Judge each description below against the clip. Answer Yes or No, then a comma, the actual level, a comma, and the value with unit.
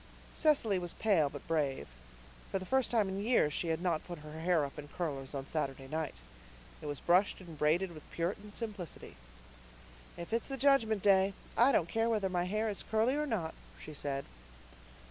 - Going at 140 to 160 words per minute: No, average, 190 wpm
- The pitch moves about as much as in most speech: No, wide, 5.9 semitones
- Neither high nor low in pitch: Yes, medium, 180 Hz